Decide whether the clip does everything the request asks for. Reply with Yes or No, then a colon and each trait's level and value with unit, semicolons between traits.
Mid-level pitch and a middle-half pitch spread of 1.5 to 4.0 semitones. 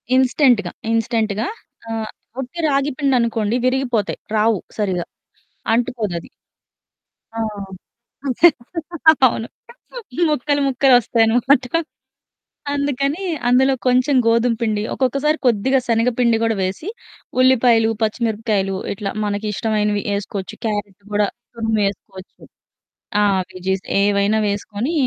No: high, 230 Hz; average, 3.7 semitones